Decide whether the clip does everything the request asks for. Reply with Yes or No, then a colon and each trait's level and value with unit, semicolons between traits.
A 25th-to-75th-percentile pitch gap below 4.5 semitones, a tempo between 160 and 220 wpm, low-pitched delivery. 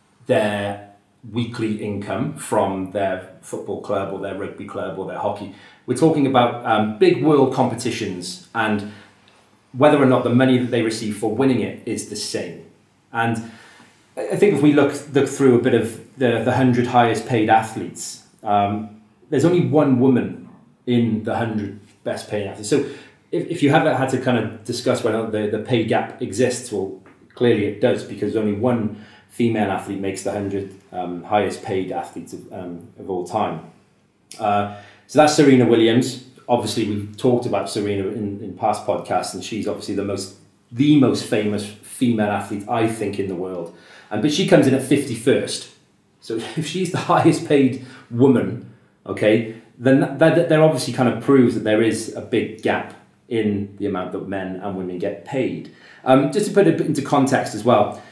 Yes: average, 4.1 semitones; average, 185 wpm; low, 110 Hz